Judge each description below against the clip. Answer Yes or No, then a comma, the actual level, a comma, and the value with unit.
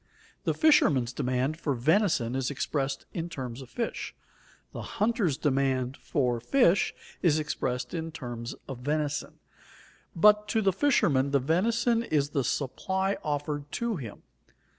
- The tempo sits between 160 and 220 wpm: No, average, 140 wpm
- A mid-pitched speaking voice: Yes, medium, 145 Hz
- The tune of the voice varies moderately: No, wide, 6.5 semitones